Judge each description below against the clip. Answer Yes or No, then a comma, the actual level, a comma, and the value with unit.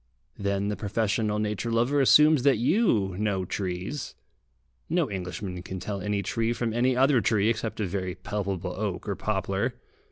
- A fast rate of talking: No, average, 160 wpm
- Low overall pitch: Yes, low, 105 Hz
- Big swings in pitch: No, average, 3.3 semitones